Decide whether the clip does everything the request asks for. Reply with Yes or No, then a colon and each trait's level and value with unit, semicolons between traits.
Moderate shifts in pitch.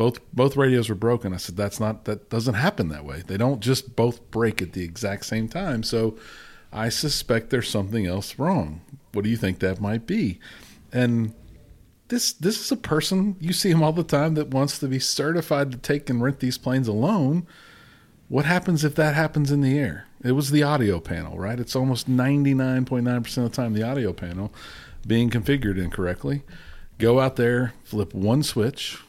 Yes: average, 4.9 semitones